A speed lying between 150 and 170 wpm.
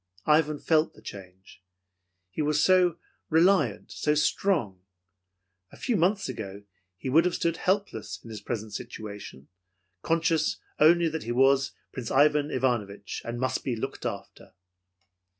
No: average, 140 wpm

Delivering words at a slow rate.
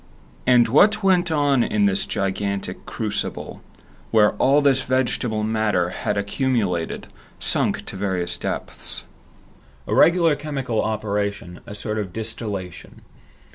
Yes: slow, 120 wpm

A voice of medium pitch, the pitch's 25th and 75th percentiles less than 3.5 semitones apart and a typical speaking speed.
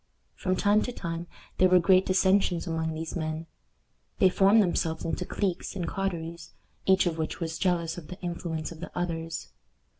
Yes: medium, 175 Hz; narrow, 2.4 semitones; average, 175 wpm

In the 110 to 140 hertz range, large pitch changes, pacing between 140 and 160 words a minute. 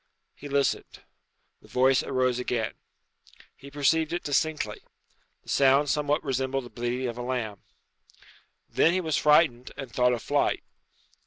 No: low, 135 Hz; average, 2.9 semitones; average, 145 wpm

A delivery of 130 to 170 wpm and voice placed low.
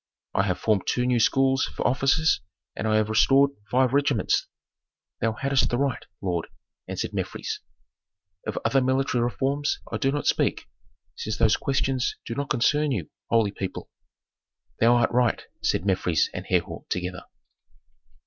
Yes: average, 150 wpm; low, 120 Hz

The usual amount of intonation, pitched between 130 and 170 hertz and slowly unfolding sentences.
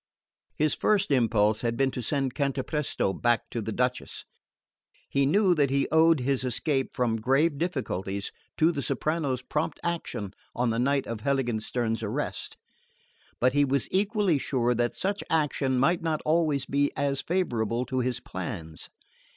No: average, 4.3 semitones; low, 135 Hz; average, 155 wpm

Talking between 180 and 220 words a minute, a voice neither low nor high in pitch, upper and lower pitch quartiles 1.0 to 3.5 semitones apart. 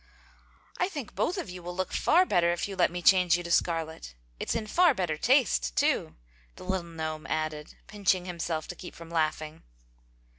Yes: average, 190 wpm; medium, 175 Hz; average, 3.1 semitones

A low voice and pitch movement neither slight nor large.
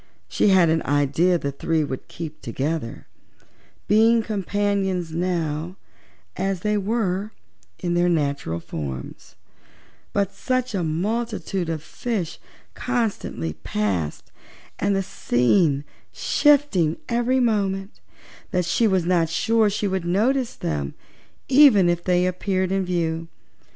No: medium, 180 Hz; average, 4.6 semitones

